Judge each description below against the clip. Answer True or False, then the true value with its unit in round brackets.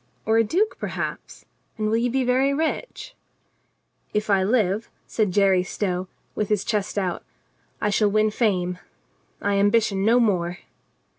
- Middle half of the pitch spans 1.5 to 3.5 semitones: True (3.1 semitones)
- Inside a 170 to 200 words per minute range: False (155 wpm)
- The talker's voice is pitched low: False (210 Hz)